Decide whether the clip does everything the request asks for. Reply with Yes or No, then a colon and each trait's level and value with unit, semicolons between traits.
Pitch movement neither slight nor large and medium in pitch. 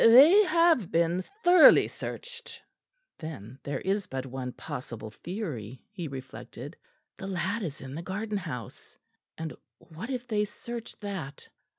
No: wide, 8.9 semitones; medium, 180 Hz